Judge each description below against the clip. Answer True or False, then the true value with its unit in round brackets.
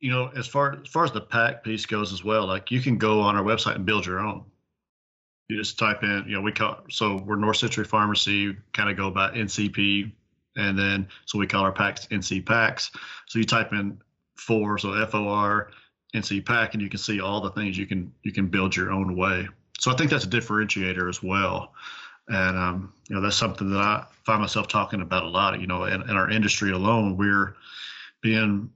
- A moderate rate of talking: False (225 wpm)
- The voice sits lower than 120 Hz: True (105 Hz)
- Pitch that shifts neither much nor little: False (1.9 semitones)